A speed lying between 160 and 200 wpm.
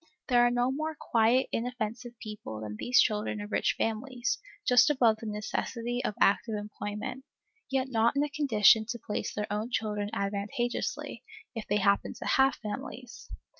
Yes: average, 165 wpm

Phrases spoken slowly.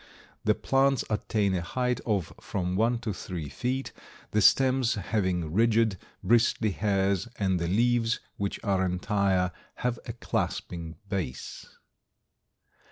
Yes: slow, 125 wpm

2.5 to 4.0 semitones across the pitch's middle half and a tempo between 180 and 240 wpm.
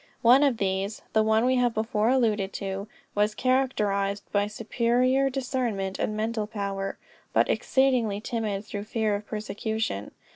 No: average, 3.1 semitones; average, 145 wpm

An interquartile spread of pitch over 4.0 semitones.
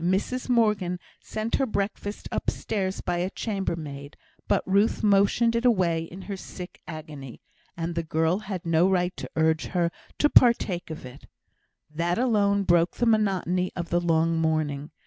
No: average, 3.7 semitones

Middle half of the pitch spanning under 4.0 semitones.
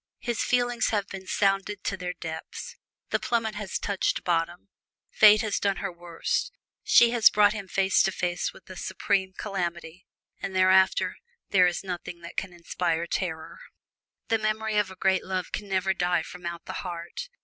Yes: average, 2.8 semitones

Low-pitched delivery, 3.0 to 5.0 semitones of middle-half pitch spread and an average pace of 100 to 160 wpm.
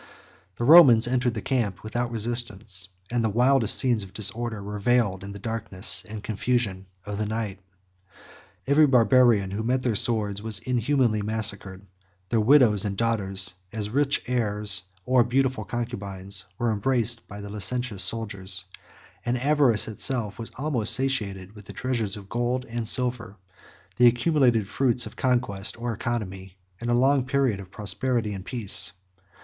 Yes: low, 115 Hz; average, 3.4 semitones; average, 155 wpm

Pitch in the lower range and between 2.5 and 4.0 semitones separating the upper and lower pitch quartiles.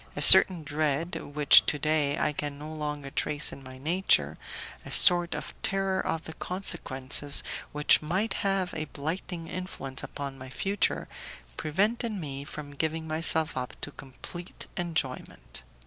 No: medium, 155 Hz; average, 3.5 semitones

